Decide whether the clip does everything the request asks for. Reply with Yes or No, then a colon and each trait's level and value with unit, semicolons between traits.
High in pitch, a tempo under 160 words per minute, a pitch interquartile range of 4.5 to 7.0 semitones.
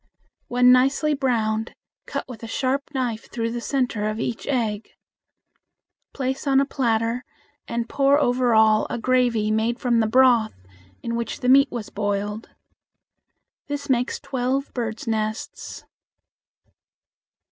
No: high, 240 Hz; slow, 135 wpm; average, 2.9 semitones